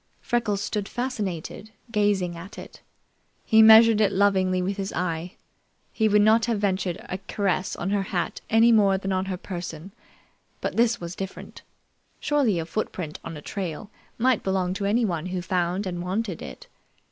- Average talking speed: Yes, average, 170 wpm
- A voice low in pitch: No, high, 195 Hz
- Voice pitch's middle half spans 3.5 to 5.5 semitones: No, average, 3.0 semitones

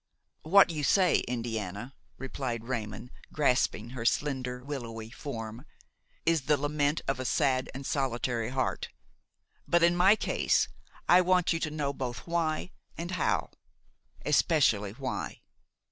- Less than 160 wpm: Yes, slow, 135 wpm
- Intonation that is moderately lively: Yes, average, 4.7 semitones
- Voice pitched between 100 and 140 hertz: Yes, low, 135 Hz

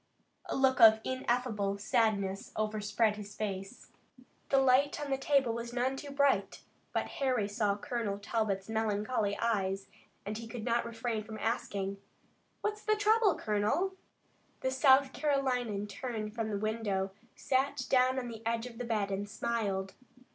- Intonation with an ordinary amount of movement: Yes, average, 4.0 semitones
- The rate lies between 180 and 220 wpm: No, average, 155 wpm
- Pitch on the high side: Yes, high, 225 Hz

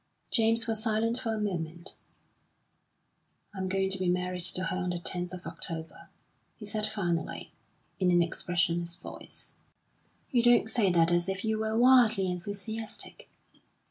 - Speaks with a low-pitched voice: No, high, 190 Hz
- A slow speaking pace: No, average, 150 wpm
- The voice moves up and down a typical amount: Yes, average, 3.8 semitones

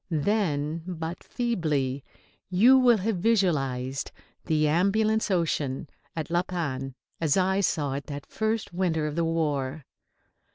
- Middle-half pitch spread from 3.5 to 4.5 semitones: No, average, 4.9 semitones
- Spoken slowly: Yes, slow, 130 wpm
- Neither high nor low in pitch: Yes, medium, 165 Hz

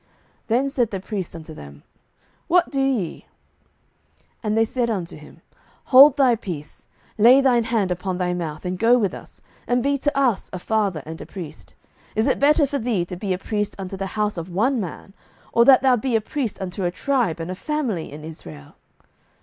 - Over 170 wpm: Yes, fast, 205 wpm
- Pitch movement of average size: No, wide, 5.9 semitones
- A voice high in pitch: Yes, high, 210 Hz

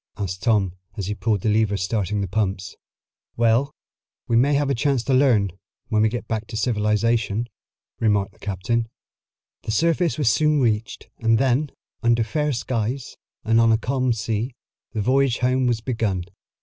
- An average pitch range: Yes, average, 3.3 semitones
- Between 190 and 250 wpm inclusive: No, average, 170 wpm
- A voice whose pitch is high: No, low, 115 Hz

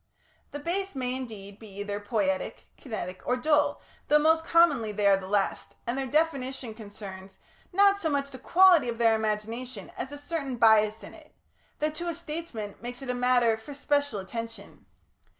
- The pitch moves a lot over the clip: Yes, wide, 5.7 semitones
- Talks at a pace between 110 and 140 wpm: No, average, 180 wpm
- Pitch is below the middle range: No, very high, 250 Hz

